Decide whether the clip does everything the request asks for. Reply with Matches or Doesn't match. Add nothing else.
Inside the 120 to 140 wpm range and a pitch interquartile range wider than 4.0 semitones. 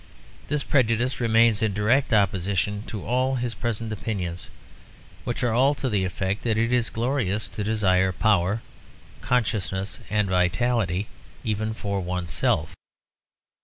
Doesn't match